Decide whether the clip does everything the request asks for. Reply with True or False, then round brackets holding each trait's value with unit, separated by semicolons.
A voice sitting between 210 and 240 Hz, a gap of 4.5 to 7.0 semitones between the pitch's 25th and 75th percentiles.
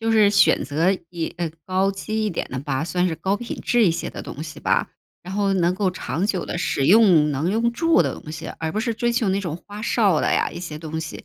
False (185 Hz; 4.8 semitones)